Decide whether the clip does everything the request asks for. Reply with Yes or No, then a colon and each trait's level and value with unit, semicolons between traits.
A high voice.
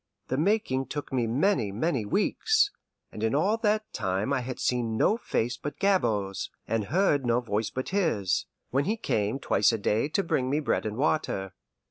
No: low, 130 Hz